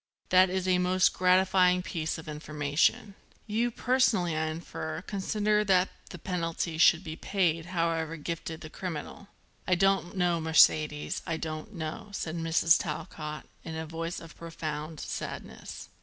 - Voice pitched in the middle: Yes, medium, 170 Hz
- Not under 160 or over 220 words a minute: No, average, 145 wpm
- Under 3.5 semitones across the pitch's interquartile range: Yes, average, 2.7 semitones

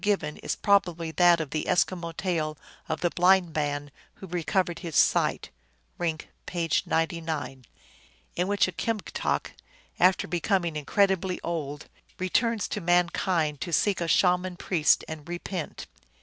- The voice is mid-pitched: Yes, medium, 175 Hz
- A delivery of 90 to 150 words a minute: Yes, average, 140 wpm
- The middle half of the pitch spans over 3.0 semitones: No, average, 2.7 semitones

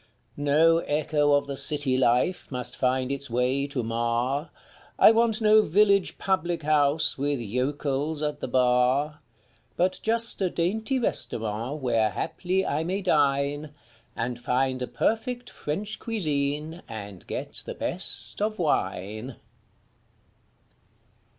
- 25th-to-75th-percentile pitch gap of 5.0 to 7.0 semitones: Yes, wide, 5.6 semitones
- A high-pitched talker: No, medium, 145 Hz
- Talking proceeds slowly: Yes, slow, 125 wpm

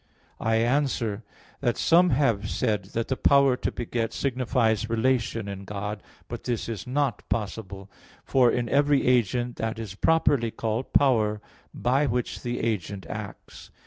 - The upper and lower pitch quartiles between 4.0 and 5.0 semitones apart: No, average, 3.1 semitones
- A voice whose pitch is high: No, low, 115 Hz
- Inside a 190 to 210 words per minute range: No, average, 145 wpm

